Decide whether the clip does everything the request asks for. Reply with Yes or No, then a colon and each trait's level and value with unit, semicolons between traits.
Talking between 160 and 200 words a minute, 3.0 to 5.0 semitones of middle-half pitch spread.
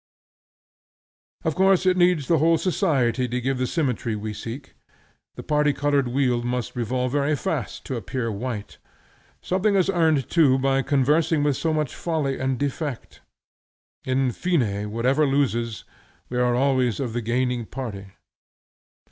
No: average, 150 wpm; average, 3.7 semitones